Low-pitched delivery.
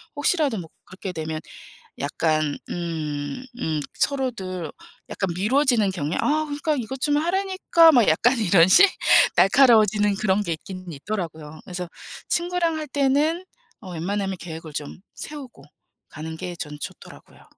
No: high, 200 Hz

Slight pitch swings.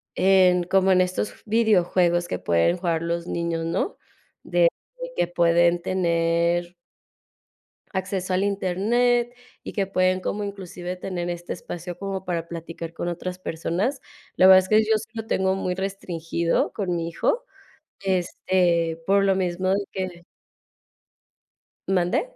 Yes: narrow, 2.0 semitones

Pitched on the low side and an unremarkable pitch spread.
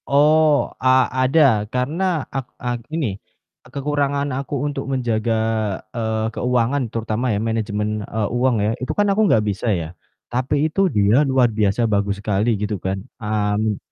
Yes: low, 120 Hz; average, 4.6 semitones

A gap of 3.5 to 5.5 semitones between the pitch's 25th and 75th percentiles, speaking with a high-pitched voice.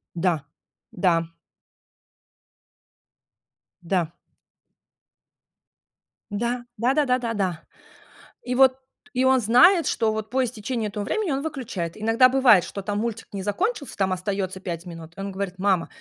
Yes: average, 5.2 semitones; high, 210 Hz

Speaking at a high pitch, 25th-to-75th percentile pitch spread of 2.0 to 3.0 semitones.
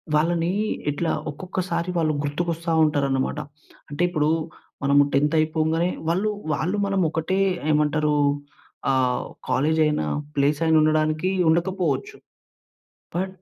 No: medium, 155 Hz; average, 2.7 semitones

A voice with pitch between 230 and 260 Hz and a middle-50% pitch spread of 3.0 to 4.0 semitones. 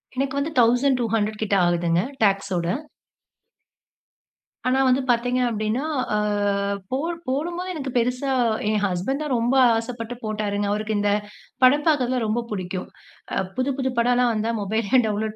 Yes: high, 235 Hz; average, 3.6 semitones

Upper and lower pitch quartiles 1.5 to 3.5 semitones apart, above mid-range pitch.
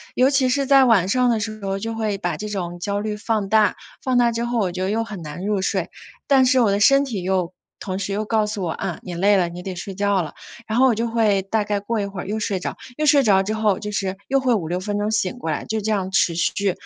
Yes: average, 3.1 semitones; high, 205 Hz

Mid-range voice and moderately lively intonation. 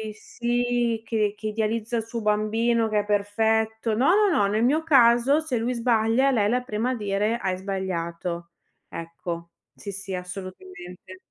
No: high, 220 Hz; average, 3.3 semitones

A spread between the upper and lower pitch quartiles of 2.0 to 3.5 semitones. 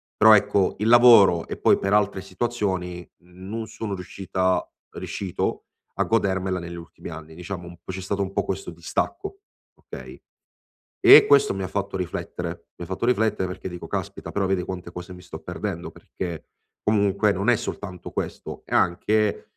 Yes: average, 2.7 semitones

